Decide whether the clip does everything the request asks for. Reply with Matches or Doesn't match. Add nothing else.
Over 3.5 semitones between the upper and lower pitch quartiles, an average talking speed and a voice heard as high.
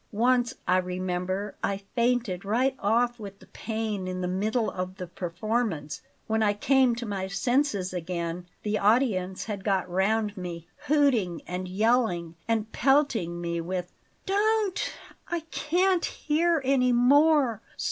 Matches